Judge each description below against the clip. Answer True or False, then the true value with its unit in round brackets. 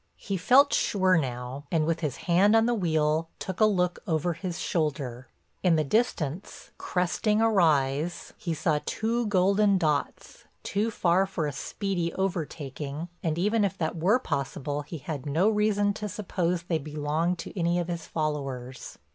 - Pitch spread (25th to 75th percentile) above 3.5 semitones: True (4.5 semitones)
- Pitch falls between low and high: True (170 Hz)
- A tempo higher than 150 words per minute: True (165 wpm)